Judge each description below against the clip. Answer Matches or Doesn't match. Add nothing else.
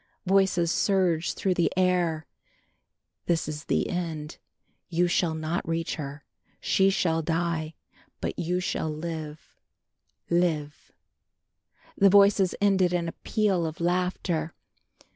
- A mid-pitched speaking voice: Matches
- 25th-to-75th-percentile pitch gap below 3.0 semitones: Matches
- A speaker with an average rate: Doesn't match